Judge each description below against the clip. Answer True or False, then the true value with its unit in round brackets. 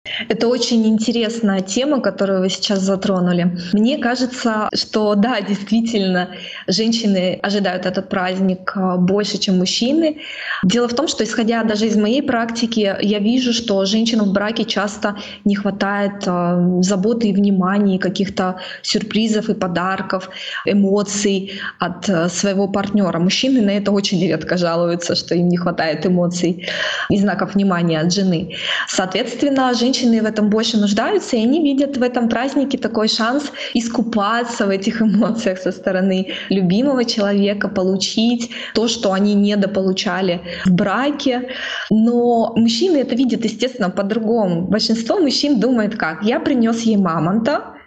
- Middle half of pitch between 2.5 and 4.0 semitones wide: True (3.6 semitones)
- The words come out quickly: False (140 wpm)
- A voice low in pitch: False (205 Hz)